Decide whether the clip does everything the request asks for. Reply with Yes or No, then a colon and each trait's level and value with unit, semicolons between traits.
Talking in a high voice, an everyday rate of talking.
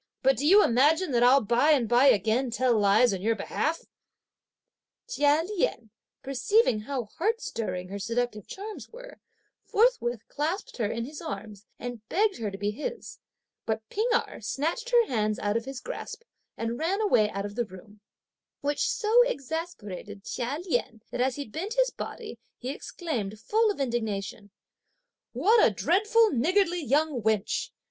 Yes: very high, 255 Hz; average, 165 wpm